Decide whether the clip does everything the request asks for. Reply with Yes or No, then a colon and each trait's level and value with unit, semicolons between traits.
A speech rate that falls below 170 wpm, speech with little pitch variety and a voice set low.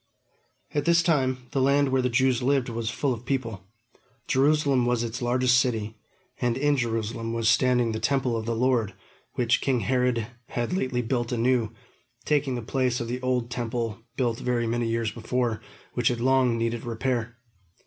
No: average, 175 wpm; narrow, 2.0 semitones; low, 120 Hz